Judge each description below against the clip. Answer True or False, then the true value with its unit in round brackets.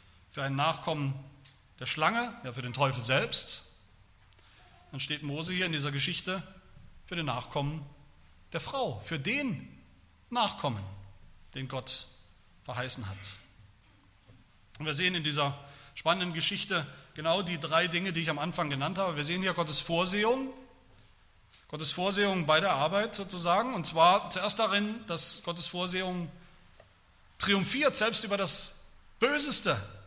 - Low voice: False (155 Hz)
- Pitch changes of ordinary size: False (6.8 semitones)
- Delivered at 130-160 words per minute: True (140 wpm)